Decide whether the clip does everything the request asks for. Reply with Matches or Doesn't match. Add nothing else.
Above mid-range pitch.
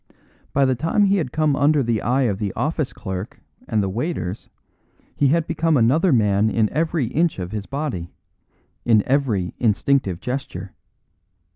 Doesn't match